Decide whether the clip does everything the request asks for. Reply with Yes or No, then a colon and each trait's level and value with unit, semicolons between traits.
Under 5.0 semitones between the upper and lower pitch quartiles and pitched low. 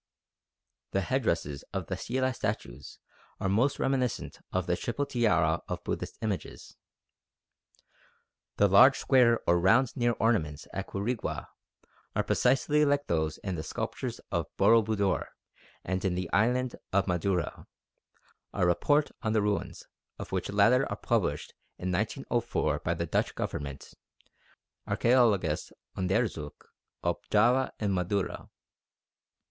No: average, 5.3 semitones; low, 105 Hz